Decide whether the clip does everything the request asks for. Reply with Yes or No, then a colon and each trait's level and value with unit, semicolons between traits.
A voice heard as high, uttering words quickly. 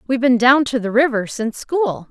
Yes: high, 245 Hz; fast, 230 wpm